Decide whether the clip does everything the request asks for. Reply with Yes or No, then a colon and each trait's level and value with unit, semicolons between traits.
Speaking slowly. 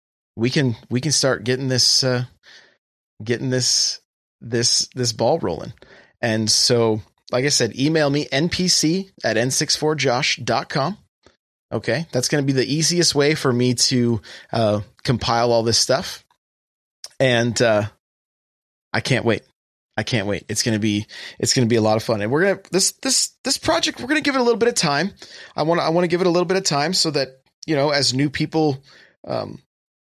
No: average, 185 wpm